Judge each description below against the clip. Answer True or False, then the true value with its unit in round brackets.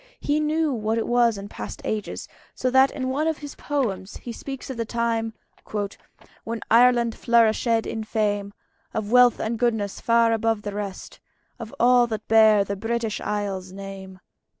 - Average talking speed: True (170 wpm)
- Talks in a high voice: True (225 Hz)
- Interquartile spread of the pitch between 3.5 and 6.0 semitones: False (2.6 semitones)